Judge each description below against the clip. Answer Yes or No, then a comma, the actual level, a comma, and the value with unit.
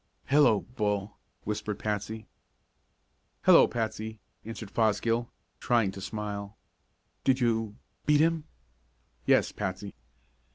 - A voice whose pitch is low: Yes, low, 110 Hz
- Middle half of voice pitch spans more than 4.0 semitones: No, narrow, 2.4 semitones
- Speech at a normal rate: No, slow, 95 wpm